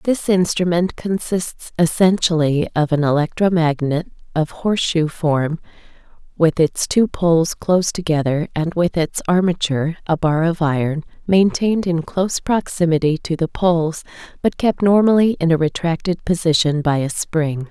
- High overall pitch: No, medium, 165 Hz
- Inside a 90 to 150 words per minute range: Yes, average, 140 wpm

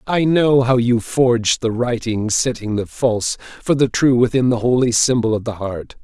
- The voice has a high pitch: No, low, 120 Hz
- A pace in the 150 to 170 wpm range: No, average, 200 wpm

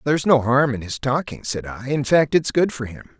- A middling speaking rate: No, fast, 265 wpm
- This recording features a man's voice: Yes, male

